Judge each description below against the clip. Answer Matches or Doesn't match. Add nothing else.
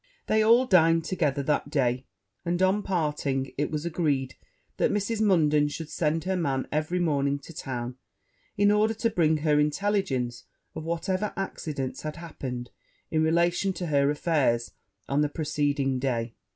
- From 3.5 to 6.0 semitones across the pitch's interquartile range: Matches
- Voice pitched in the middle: Matches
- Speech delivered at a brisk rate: Doesn't match